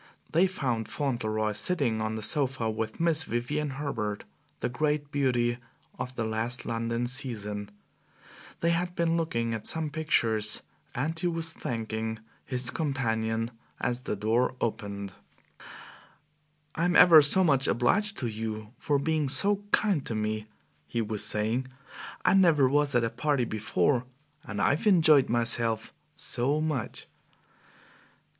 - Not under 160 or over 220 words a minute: No, slow, 135 wpm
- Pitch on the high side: No, low, 125 Hz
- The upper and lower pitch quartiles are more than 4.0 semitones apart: Yes, average, 5.3 semitones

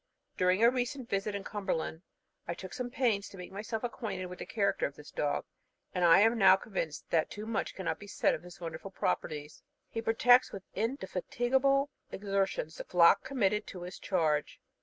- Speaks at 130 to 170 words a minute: No, average, 185 wpm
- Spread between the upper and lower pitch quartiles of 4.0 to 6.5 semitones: Yes, average, 4.3 semitones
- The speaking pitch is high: Yes, high, 195 Hz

